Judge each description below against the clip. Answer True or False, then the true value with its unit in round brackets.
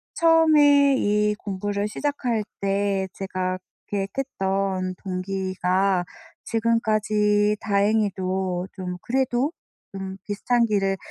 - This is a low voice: False (205 Hz)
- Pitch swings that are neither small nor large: True (3.1 semitones)